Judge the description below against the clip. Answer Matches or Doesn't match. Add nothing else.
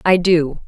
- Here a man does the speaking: Doesn't match